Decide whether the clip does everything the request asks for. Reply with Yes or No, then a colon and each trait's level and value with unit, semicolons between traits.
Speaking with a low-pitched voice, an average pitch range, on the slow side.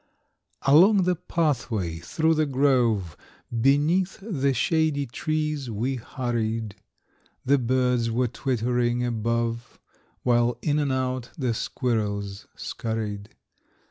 Yes: low, 125 Hz; average, 3.9 semitones; slow, 105 wpm